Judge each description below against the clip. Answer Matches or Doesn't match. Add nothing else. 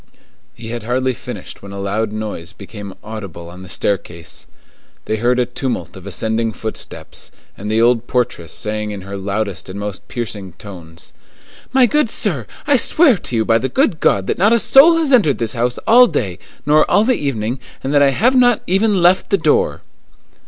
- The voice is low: Matches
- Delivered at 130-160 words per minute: Doesn't match